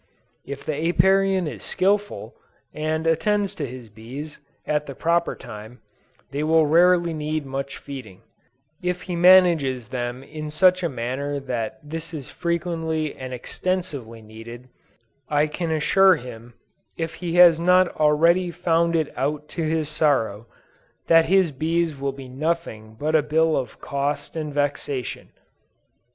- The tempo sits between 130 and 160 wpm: Yes, average, 145 wpm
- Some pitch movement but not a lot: Yes, average, 4.0 semitones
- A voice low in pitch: No, medium, 155 Hz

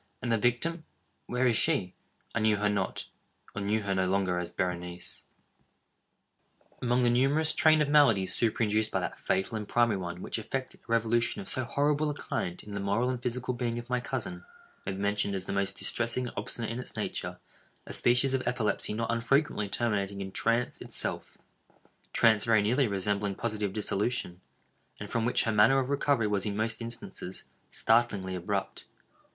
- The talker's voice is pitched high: No, low, 115 Hz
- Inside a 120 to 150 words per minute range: No, average, 175 wpm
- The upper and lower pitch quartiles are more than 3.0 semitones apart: Yes, average, 3.6 semitones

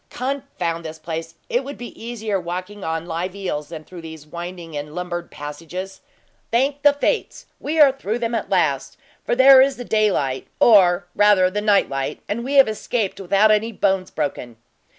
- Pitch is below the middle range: No, high, 190 Hz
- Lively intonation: Yes, wide, 6.1 semitones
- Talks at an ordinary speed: Yes, average, 175 wpm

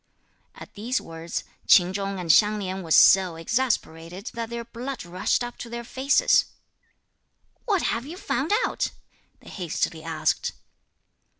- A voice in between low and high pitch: No, high, 205 Hz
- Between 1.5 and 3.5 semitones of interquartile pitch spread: No, wide, 5.5 semitones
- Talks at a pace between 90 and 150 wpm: Yes, average, 140 wpm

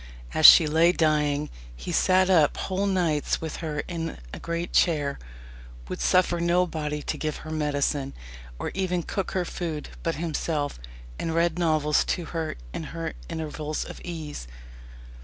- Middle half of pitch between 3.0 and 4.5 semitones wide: No, narrow, 2.5 semitones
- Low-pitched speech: No, medium, 160 Hz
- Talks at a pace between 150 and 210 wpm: Yes, average, 155 wpm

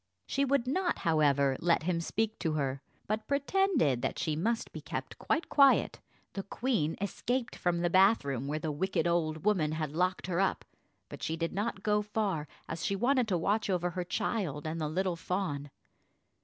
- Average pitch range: No, wide, 5.7 semitones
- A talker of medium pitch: Yes, medium, 180 Hz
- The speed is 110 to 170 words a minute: No, average, 190 wpm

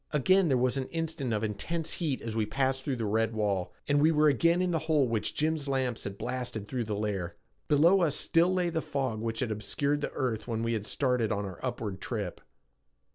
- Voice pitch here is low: Yes, low, 130 Hz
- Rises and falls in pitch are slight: No, wide, 5.6 semitones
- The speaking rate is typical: No, fast, 225 wpm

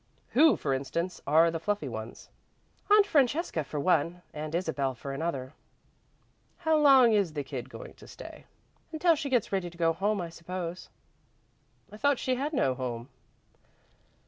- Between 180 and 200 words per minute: No, average, 160 wpm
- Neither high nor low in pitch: Yes, medium, 170 Hz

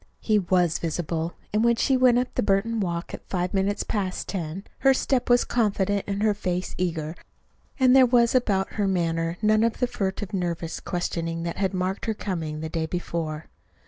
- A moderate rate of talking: Yes, average, 190 wpm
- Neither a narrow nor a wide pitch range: Yes, average, 4.2 semitones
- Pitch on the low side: No, high, 190 Hz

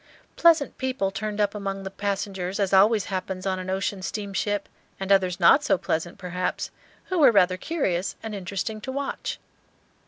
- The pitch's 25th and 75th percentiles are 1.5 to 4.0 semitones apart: Yes, narrow, 2.4 semitones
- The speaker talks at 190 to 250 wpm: No, average, 165 wpm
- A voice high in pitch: Yes, high, 195 Hz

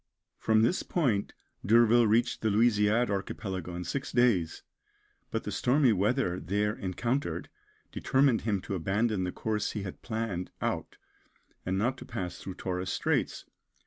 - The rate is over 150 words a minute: No, average, 145 wpm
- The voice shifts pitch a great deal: No, average, 4.1 semitones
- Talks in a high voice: No, low, 105 Hz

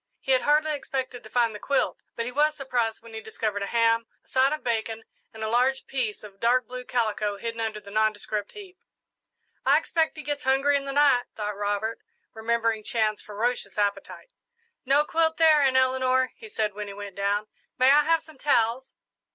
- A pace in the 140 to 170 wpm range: No, average, 200 wpm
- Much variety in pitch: No, average, 4.1 semitones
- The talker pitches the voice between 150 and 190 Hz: No, high, 235 Hz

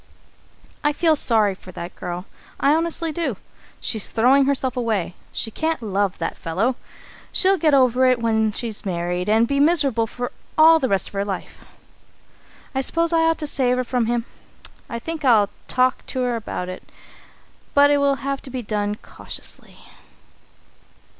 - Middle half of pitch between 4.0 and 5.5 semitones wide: Yes, average, 5.2 semitones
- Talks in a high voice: Yes, very high, 250 Hz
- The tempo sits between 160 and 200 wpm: Yes, average, 165 wpm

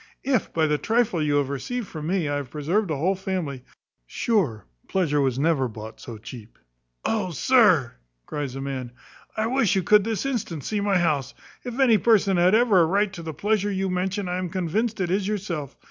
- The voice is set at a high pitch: No, medium, 180 Hz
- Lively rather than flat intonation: Yes, wide, 6.3 semitones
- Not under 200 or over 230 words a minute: Yes, fast, 205 wpm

